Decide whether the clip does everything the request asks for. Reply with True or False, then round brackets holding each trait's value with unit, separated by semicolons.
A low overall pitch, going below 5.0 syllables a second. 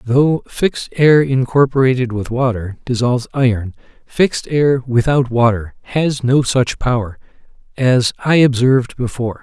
True (125 Hz; 4.6 syllables/s)